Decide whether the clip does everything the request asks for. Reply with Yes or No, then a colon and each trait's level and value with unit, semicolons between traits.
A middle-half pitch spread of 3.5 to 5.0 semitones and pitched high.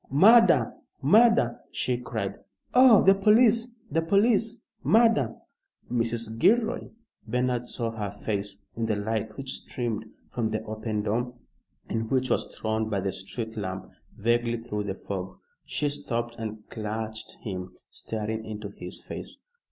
No: average, 4.1 semitones; low, 115 Hz